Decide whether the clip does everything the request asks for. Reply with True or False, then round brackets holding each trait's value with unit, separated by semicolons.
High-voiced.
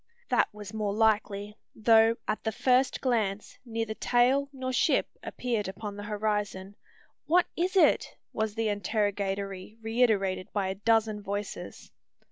True (215 Hz)